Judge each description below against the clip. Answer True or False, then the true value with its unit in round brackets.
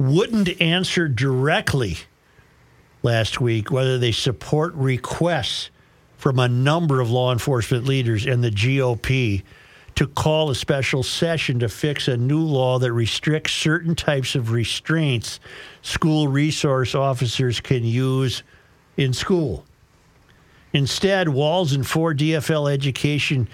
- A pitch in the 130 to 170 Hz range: True (135 Hz)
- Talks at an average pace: False (120 wpm)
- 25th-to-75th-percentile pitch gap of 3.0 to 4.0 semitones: True (3.7 semitones)